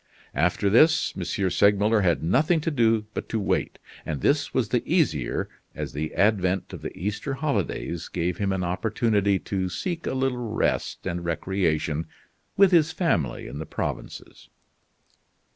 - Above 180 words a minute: No, average, 155 wpm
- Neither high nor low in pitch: No, low, 100 Hz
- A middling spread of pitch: No, wide, 6.7 semitones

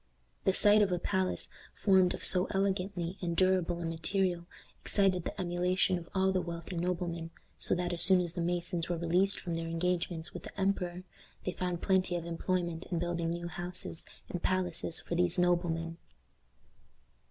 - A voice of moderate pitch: Yes, medium, 175 Hz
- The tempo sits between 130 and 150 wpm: No, average, 175 wpm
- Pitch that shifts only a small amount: Yes, narrow, 1.6 semitones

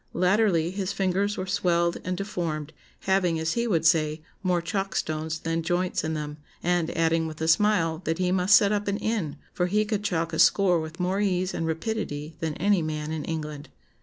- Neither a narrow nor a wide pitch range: Yes, average, 3.4 semitones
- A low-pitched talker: No, medium, 175 Hz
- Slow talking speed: No, average, 200 wpm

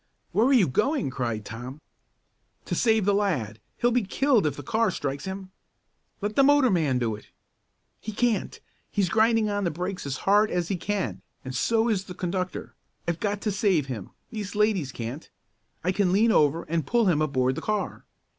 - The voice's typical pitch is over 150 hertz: Yes, high, 190 Hz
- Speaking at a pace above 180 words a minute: Yes, average, 190 wpm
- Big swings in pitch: Yes, wide, 6.7 semitones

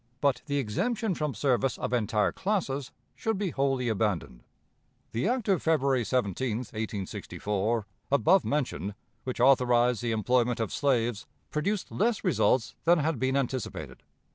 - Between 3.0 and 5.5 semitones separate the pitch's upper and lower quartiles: Yes, average, 5.2 semitones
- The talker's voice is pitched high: No, low, 130 Hz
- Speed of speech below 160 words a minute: Yes, average, 140 wpm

